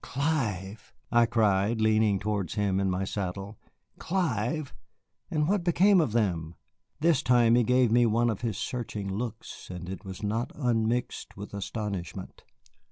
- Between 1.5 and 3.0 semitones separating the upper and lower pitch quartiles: No, average, 3.8 semitones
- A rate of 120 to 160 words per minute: Yes, average, 150 wpm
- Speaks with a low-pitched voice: Yes, low, 110 Hz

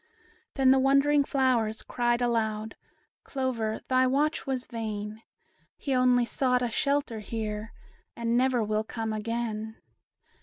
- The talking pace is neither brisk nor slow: No, slow, 125 wpm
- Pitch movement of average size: Yes, average, 3.0 semitones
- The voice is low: No, high, 240 Hz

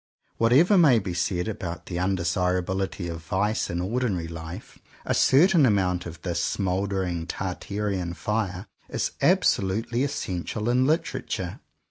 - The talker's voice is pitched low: Yes, very low, 95 Hz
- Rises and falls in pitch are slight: No, average, 4.3 semitones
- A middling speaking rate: No, slow, 125 wpm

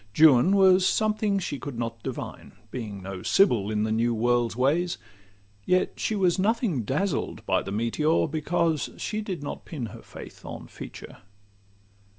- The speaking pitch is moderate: Yes, medium, 150 Hz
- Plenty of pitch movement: Yes, wide, 8.2 semitones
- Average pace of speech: Yes, average, 160 wpm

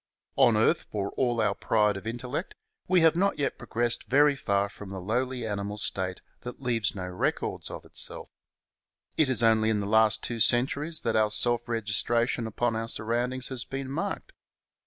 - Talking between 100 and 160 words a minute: No, average, 180 wpm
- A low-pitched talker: Yes, low, 115 Hz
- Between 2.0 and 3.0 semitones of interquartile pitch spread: No, average, 3.4 semitones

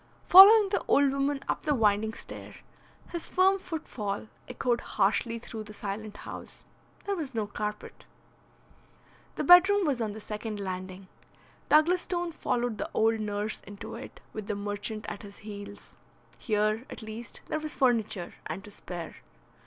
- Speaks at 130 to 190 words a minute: Yes, average, 155 wpm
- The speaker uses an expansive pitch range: Yes, wide, 5.9 semitones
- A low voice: No, high, 220 Hz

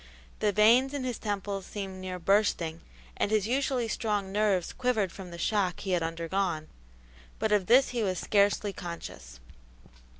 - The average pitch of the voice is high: Yes, high, 200 Hz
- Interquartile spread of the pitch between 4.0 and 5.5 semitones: No, average, 3.1 semitones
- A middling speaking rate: Yes, average, 160 wpm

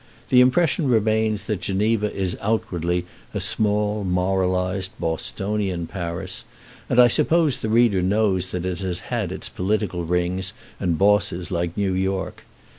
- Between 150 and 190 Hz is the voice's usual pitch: No, very low, 95 Hz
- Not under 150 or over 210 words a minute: No, average, 140 wpm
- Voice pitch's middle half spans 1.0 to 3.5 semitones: Yes, average, 3.0 semitones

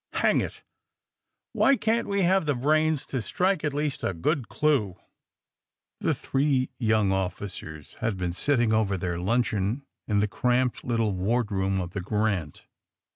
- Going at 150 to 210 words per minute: Yes, average, 155 wpm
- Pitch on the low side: Yes, low, 115 Hz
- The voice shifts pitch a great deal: Yes, wide, 7.0 semitones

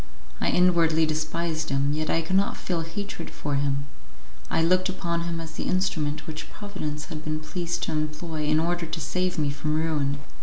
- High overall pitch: No, medium, 160 Hz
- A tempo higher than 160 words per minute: Yes, average, 190 wpm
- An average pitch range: No, narrow, 2.0 semitones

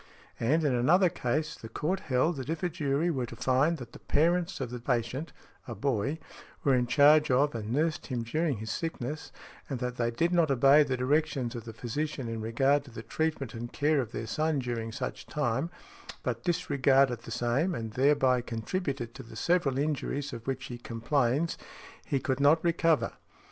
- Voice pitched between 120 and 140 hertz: Yes, low, 135 Hz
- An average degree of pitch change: Yes, average, 4.3 semitones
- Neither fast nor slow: Yes, average, 190 wpm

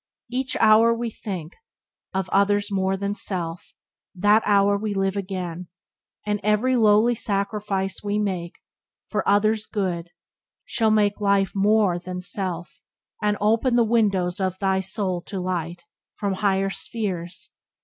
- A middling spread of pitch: No, narrow, 2.2 semitones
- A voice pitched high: Yes, high, 200 Hz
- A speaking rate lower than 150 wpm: Yes, average, 140 wpm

